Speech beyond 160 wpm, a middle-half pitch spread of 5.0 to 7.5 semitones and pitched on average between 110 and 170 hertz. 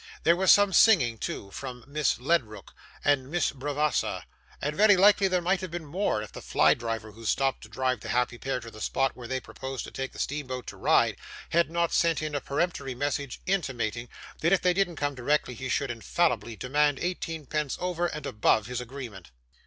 Yes: average, 200 wpm; wide, 5.5 semitones; medium, 140 Hz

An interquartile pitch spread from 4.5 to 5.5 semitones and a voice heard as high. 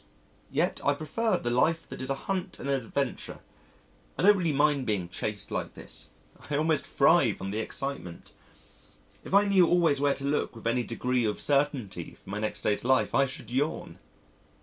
No: average, 5.2 semitones; medium, 140 Hz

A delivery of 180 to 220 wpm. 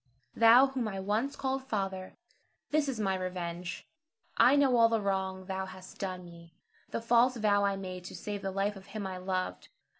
Yes: average, 190 wpm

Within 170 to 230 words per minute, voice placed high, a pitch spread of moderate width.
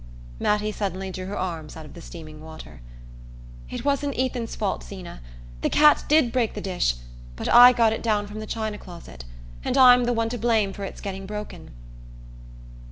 Yes: average, 185 wpm; high, 210 Hz; average, 4.3 semitones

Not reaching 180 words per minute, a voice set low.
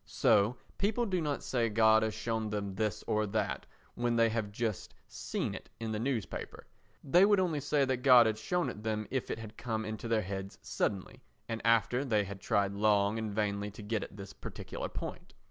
No: fast, 205 wpm; low, 110 Hz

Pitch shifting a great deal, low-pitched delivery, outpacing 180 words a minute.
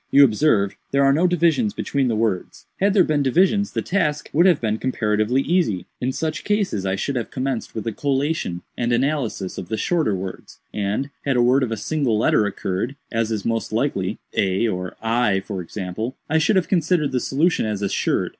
Yes: wide, 6.4 semitones; low, 125 Hz; average, 200 wpm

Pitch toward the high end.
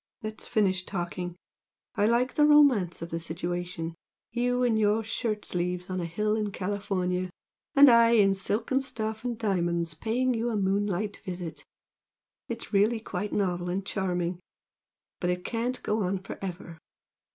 Yes: high, 200 Hz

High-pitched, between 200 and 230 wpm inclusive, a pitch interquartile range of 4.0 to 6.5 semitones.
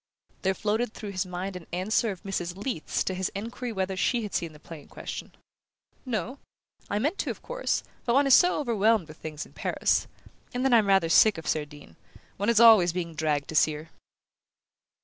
Yes: high, 195 Hz; fast, 205 wpm; wide, 5.5 semitones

